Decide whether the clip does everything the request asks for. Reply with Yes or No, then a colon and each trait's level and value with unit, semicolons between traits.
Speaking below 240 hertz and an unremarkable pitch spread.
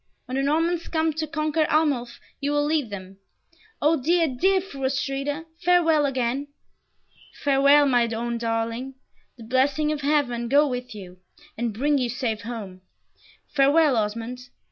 No: very high, 275 Hz; average, 4.2 semitones